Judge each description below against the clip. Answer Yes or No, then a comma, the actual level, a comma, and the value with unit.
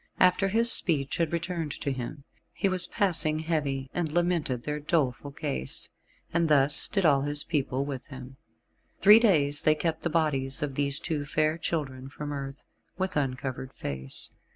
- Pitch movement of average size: Yes, average, 3.7 semitones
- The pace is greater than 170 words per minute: No, average, 165 wpm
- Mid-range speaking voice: Yes, medium, 150 Hz